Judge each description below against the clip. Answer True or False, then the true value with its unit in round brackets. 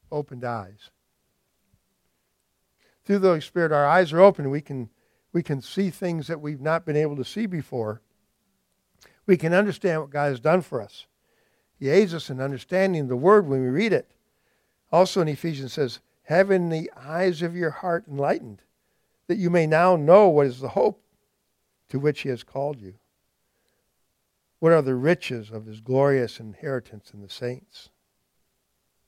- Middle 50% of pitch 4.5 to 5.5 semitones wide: True (5.1 semitones)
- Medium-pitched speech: True (150 Hz)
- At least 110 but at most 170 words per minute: True (165 wpm)